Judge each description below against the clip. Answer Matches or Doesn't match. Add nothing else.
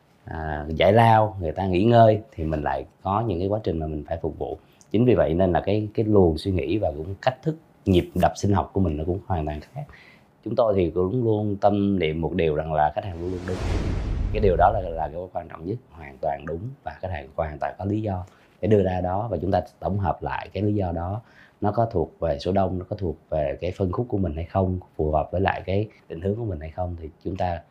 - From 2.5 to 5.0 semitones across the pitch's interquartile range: Matches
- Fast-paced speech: Matches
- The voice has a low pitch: Matches